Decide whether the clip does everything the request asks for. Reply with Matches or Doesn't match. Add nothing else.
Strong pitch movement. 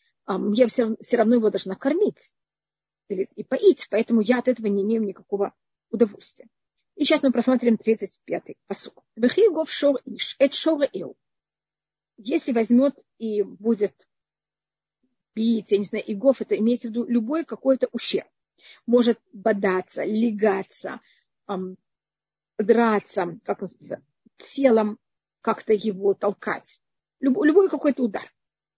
Doesn't match